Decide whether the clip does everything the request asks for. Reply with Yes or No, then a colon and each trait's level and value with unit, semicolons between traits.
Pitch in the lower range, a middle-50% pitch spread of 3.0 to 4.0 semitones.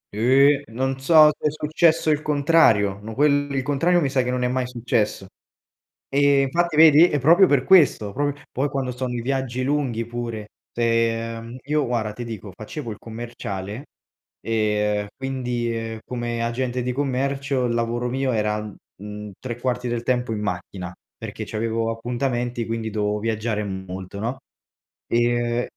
Yes: low, 120 Hz; average, 3.3 semitones